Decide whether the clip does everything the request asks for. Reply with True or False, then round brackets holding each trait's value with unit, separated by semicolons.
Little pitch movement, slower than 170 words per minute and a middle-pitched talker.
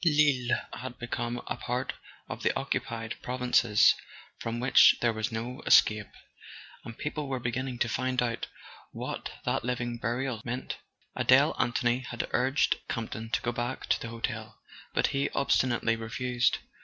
False (1.8 semitones; 155 wpm; 120 Hz)